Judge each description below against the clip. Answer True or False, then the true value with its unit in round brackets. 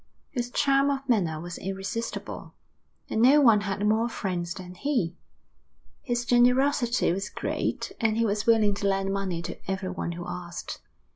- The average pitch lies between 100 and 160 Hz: False (210 Hz)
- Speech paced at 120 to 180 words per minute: True (155 wpm)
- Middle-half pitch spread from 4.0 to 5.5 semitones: True (4.6 semitones)